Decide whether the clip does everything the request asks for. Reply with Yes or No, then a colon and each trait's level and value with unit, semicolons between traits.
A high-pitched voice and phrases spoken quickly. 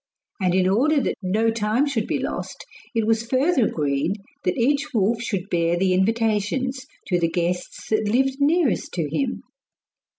No: high, 220 Hz; average, 165 wpm